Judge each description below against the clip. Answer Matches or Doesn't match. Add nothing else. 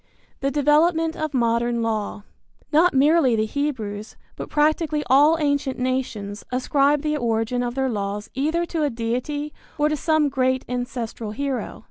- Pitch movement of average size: Matches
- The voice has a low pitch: Doesn't match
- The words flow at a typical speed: Matches